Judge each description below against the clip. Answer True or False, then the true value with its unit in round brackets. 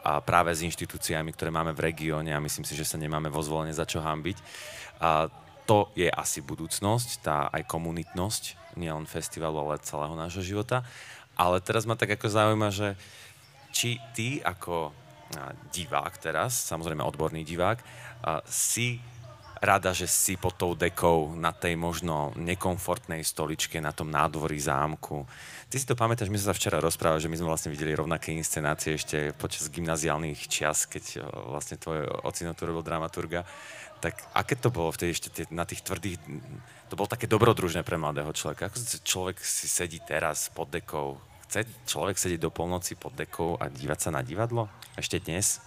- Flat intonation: False (4.7 semitones)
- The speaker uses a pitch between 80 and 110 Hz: True (85 Hz)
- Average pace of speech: False (170 wpm)